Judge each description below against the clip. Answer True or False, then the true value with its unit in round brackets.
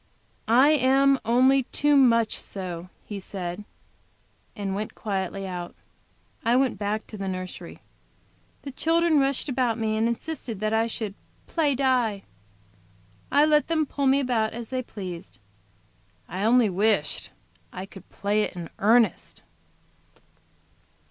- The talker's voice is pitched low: False (225 Hz)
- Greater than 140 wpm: False (135 wpm)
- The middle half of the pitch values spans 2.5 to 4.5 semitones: False (5.1 semitones)